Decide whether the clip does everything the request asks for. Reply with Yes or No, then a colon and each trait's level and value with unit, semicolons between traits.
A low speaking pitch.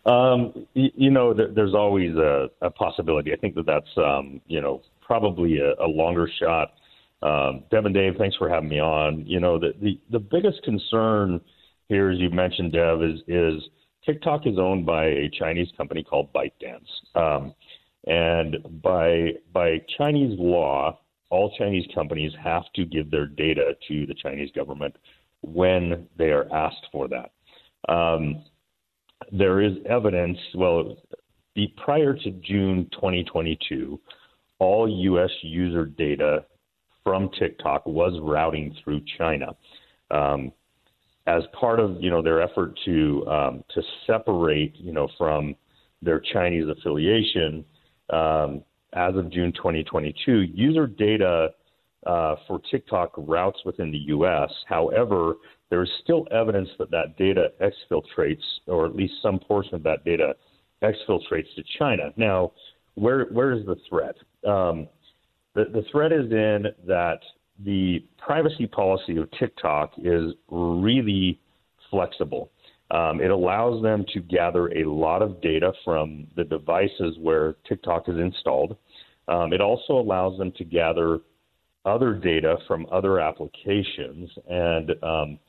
Yes: very low, 90 Hz